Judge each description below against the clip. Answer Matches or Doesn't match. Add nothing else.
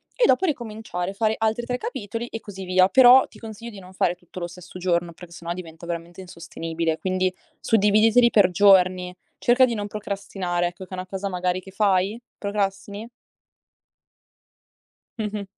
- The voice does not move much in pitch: Doesn't match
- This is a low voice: Doesn't match